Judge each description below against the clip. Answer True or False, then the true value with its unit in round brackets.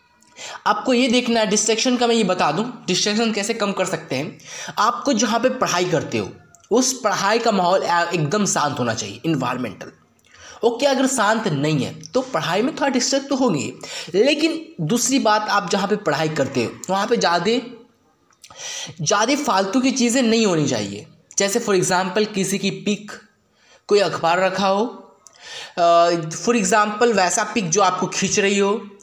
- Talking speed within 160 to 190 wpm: True (165 wpm)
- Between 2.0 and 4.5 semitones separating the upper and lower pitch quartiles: False (5.0 semitones)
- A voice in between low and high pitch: False (205 Hz)